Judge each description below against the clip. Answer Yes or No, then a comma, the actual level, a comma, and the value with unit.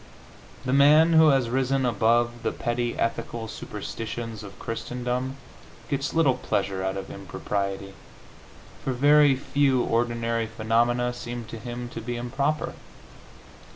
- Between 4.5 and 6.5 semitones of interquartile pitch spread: No, narrow, 2.6 semitones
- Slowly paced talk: Yes, slow, 125 wpm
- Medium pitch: No, low, 120 Hz